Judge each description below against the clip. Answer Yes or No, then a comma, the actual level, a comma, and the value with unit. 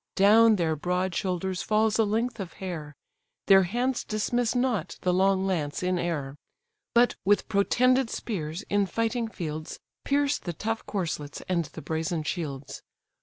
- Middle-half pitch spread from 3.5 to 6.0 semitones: Yes, average, 5.0 semitones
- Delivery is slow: No, average, 150 wpm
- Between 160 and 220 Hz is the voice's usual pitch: Yes, high, 190 Hz